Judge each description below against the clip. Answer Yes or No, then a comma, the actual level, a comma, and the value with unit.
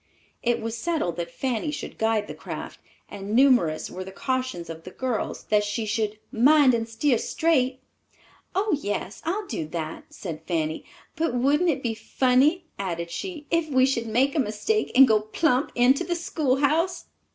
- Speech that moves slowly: No, average, 175 wpm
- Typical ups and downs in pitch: No, wide, 6.1 semitones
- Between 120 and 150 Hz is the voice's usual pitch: No, very high, 250 Hz